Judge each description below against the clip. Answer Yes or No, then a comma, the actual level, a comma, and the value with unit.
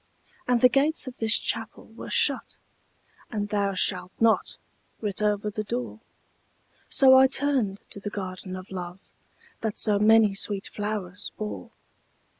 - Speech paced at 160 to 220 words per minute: No, average, 145 wpm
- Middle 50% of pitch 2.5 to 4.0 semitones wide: Yes, average, 2.8 semitones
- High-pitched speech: Yes, high, 210 Hz